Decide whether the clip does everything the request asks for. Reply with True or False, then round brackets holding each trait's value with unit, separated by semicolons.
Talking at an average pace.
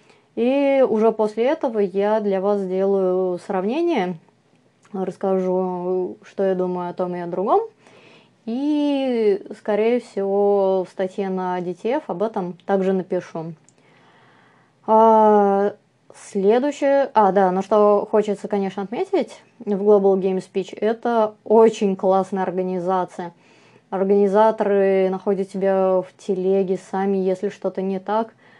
True (120 wpm)